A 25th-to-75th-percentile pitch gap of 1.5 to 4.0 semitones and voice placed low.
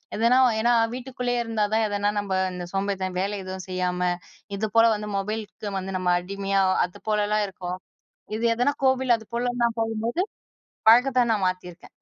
No: average, 3.7 semitones; high, 210 Hz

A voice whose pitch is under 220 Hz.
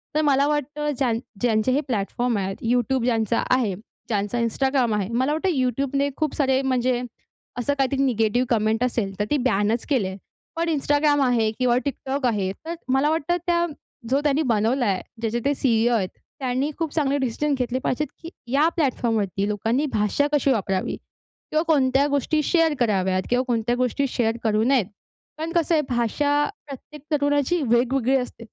No: very high, 255 Hz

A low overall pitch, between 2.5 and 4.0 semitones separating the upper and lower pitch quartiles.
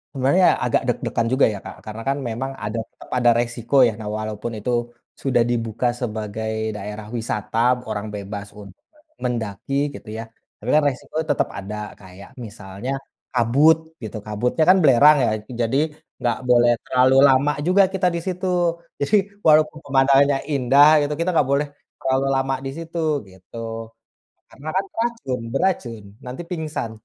No: low, 125 Hz; average, 4.7 semitones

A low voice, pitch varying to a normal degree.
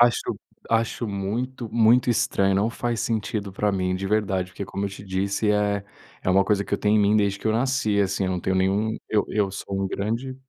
No: low, 105 Hz; narrow, 2.3 semitones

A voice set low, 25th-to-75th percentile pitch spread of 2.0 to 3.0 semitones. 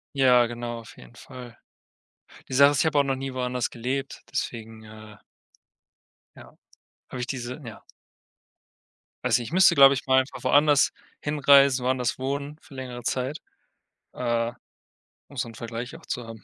Yes: low, 125 Hz; narrow, 2.6 semitones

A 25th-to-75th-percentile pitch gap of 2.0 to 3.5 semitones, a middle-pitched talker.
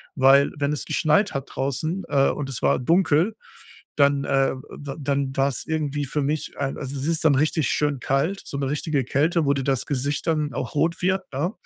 Yes: narrow, 2.4 semitones; medium, 145 Hz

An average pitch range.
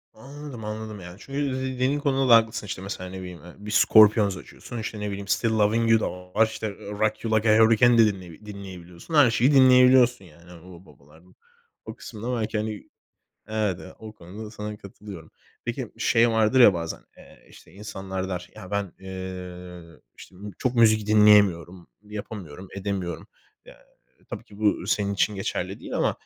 Yes: average, 3.2 semitones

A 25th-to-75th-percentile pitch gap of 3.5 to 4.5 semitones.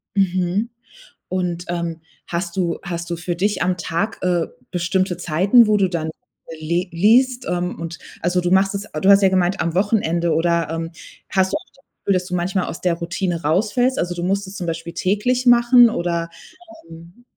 No: average, 2.7 semitones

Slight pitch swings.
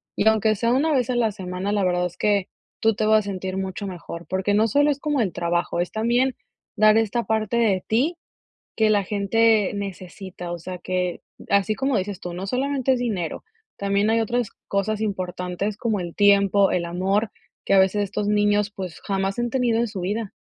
No: average, 3.1 semitones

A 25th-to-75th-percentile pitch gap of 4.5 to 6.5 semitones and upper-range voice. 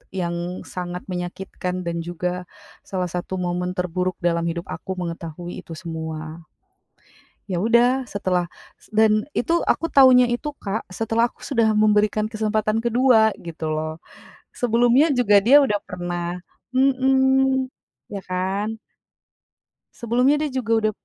Yes: average, 5.3 semitones; high, 200 Hz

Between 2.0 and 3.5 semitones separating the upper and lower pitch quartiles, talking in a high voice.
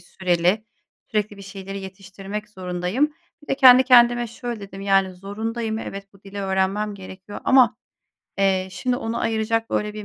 Yes: average, 2.8 semitones; high, 205 Hz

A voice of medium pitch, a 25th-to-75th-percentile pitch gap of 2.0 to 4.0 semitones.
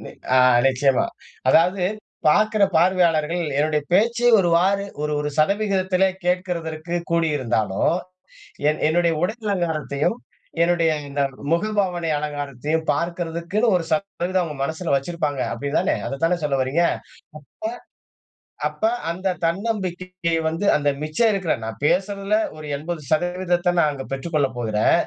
Yes: medium, 170 Hz; average, 3.6 semitones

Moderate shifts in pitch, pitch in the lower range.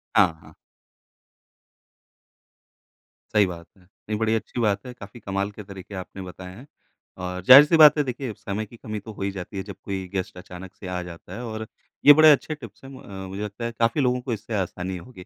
Yes: average, 4.2 semitones; low, 105 Hz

